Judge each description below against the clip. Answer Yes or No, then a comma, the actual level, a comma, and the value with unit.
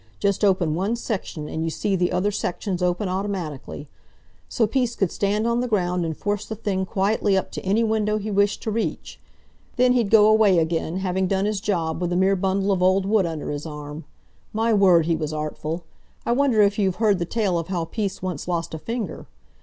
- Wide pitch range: No, average, 3.4 semitones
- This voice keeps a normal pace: No, fast, 215 wpm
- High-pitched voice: Yes, high, 195 Hz